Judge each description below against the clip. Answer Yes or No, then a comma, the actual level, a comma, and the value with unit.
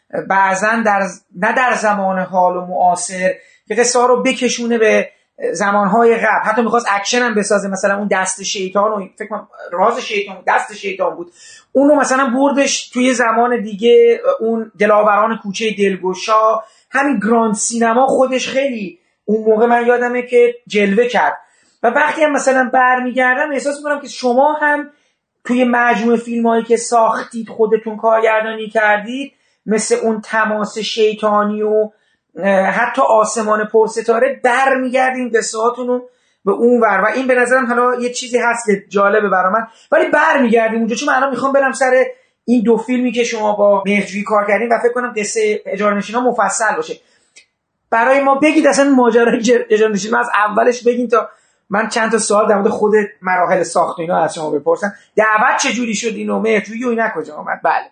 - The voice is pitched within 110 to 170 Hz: No, high, 225 Hz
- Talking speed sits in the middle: No, fast, 170 wpm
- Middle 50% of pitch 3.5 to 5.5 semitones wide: No, average, 3.1 semitones